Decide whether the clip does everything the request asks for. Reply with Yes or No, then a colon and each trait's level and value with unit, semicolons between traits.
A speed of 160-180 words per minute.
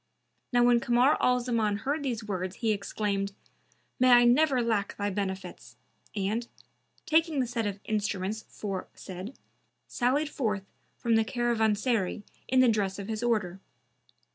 No: average, 140 wpm